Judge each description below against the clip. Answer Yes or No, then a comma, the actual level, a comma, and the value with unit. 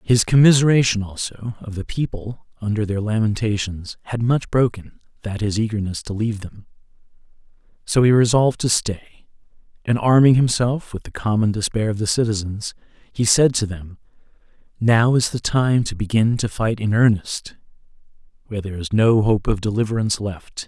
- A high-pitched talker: No, low, 110 Hz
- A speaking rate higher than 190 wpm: No, average, 160 wpm